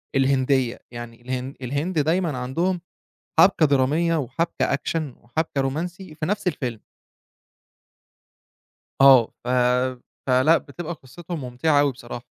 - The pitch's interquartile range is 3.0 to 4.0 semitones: No, average, 4.4 semitones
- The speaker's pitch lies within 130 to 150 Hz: Yes, medium, 140 Hz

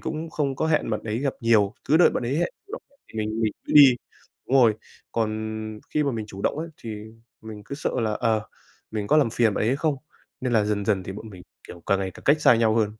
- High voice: No, low, 115 Hz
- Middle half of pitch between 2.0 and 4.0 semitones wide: No, average, 4.7 semitones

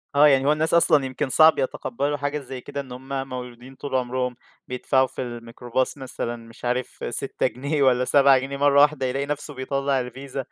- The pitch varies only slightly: Yes, narrow, 2.0 semitones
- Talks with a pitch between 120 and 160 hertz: Yes, low, 135 Hz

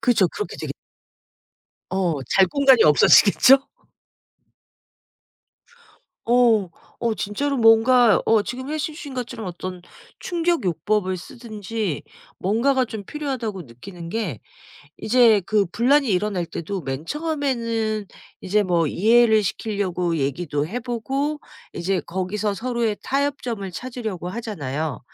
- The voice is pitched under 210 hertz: No, high, 215 Hz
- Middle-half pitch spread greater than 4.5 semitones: Yes, average, 5.2 semitones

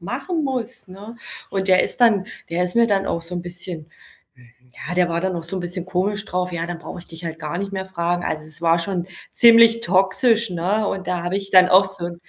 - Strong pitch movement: No, average, 2.7 semitones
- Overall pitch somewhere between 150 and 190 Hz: Yes, medium, 185 Hz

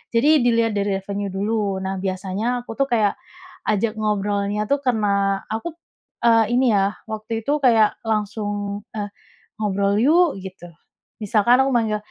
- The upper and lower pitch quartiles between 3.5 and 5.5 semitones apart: No, narrow, 2.5 semitones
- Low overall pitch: No, high, 210 Hz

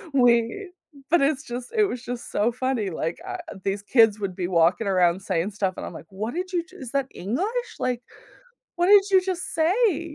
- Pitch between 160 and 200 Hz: No, high, 245 Hz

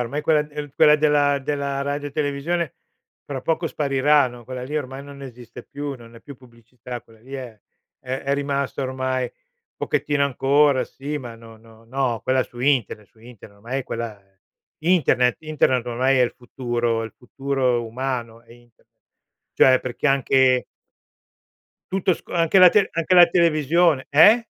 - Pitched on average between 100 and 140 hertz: Yes, low, 135 Hz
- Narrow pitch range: No, average, 3.2 semitones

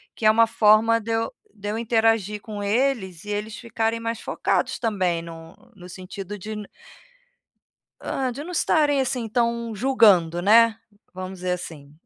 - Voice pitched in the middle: No, high, 215 Hz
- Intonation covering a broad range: No, average, 3.4 semitones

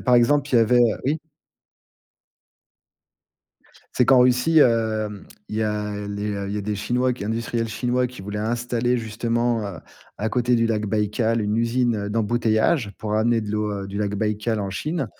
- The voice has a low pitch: Yes, low, 115 Hz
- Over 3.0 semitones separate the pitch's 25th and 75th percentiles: No, narrow, 2.5 semitones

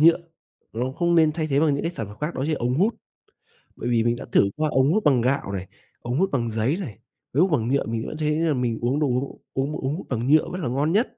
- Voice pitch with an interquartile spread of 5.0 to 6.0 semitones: No, average, 4.6 semitones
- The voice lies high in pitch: No, medium, 140 Hz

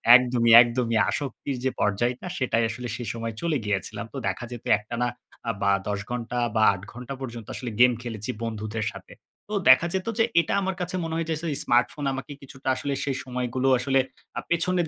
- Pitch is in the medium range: No, low, 125 Hz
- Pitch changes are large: No, average, 3.1 semitones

